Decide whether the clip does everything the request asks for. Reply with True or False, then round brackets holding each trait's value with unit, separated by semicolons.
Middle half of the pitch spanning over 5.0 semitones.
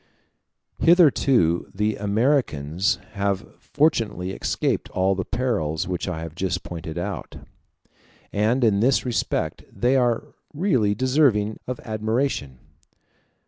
True (5.6 semitones)